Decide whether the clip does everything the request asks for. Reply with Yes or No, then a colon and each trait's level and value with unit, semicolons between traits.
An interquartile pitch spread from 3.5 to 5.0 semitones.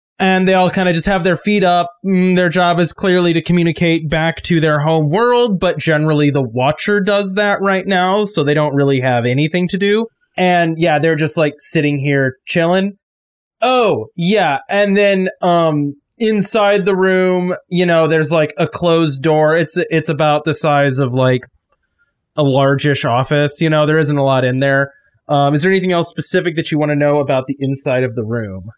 Yes: average, 4.1 semitones